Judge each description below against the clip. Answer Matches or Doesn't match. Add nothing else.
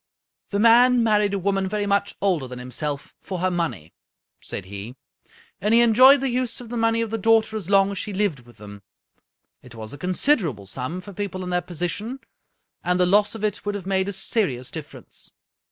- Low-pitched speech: Doesn't match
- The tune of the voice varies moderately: Doesn't match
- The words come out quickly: Matches